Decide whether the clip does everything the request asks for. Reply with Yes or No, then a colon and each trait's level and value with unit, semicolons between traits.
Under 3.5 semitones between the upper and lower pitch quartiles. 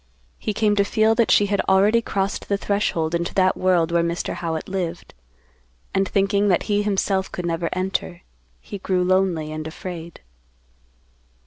Yes: average, 2.9 semitones